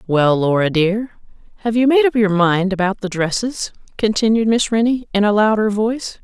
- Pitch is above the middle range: Yes, high, 210 Hz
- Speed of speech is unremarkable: Yes, average, 185 wpm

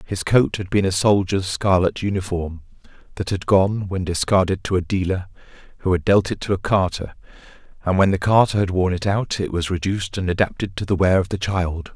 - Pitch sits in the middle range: No, very low, 95 Hz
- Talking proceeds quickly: Yes, fast, 210 wpm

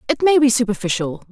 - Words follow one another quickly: No, average, 185 wpm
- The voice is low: No, high, 230 Hz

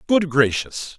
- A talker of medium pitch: Yes, medium, 155 Hz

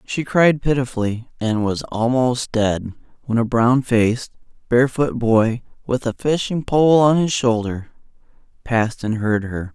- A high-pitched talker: No, low, 120 Hz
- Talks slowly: No, average, 150 wpm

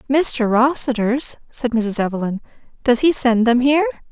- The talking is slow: Yes, slow, 130 wpm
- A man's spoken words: No, female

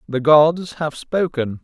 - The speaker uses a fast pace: No, average, 145 wpm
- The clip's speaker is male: Yes, male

